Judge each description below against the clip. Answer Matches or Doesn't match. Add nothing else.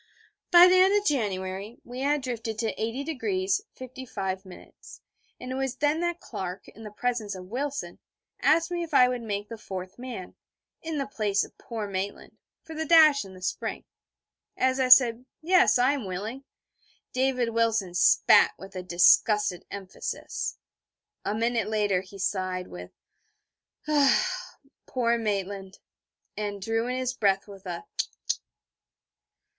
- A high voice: Matches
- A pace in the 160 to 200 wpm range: Doesn't match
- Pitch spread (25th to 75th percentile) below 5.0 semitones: Doesn't match